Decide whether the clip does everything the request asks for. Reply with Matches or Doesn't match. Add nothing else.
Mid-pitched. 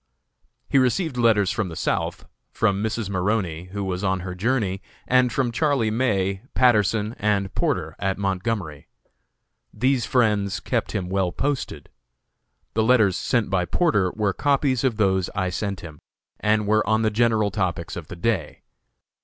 Doesn't match